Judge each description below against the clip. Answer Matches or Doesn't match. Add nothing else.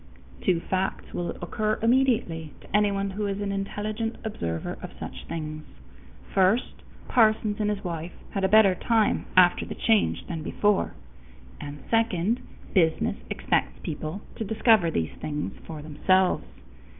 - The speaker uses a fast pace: Doesn't match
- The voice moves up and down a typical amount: Matches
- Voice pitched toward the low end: Doesn't match